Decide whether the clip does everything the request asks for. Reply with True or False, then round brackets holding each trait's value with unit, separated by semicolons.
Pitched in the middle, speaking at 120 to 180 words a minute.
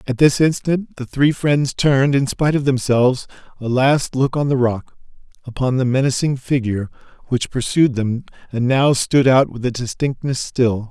False (130 Hz; 175 wpm)